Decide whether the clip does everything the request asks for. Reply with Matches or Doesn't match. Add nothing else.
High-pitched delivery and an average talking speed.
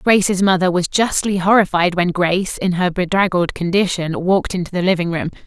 Doesn't match